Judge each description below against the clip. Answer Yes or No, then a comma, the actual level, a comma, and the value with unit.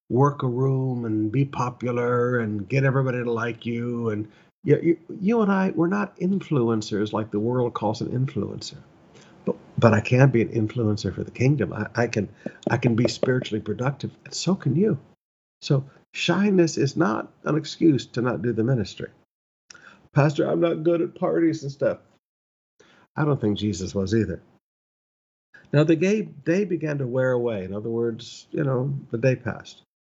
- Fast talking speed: No, average, 180 wpm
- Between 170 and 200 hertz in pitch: No, low, 125 Hz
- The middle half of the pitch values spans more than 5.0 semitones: Yes, wide, 5.6 semitones